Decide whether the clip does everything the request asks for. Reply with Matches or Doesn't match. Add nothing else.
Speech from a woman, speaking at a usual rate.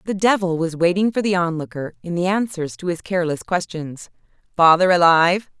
Matches